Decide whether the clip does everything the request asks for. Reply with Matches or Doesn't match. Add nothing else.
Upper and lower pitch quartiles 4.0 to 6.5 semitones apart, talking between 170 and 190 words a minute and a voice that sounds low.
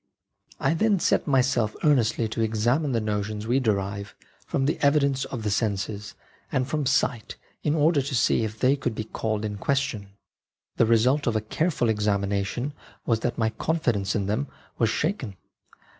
Matches